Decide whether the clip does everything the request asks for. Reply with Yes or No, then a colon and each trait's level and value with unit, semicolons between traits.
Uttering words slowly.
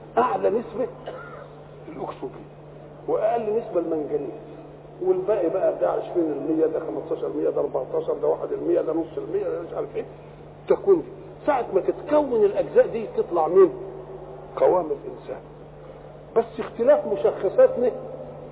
Yes: slow, 115 wpm